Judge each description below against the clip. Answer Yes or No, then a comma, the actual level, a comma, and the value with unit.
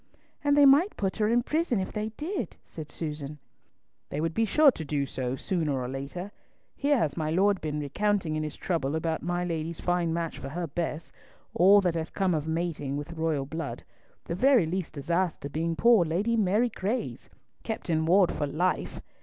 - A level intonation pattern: No, average, 4.8 semitones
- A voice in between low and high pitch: Yes, medium, 170 Hz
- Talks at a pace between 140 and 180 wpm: No, average, 195 wpm